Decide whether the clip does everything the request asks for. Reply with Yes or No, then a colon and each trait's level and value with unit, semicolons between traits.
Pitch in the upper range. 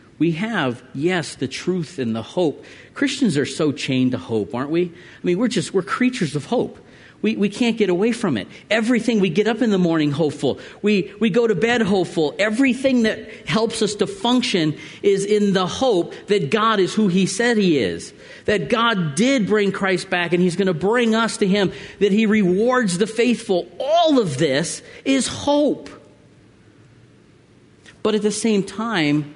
Yes: high, 200 Hz